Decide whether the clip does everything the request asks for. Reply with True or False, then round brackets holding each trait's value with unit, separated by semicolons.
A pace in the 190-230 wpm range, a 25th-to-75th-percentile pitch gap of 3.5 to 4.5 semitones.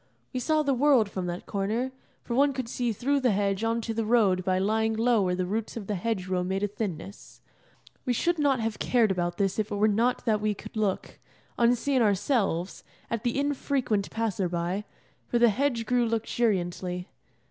True (200 wpm; 3.8 semitones)